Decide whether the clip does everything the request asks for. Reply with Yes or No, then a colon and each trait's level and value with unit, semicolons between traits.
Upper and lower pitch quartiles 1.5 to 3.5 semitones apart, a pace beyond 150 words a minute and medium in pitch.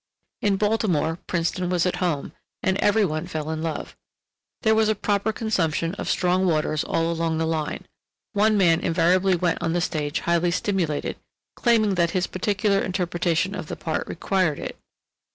Yes: average, 3.2 semitones; average, 170 wpm; medium, 175 Hz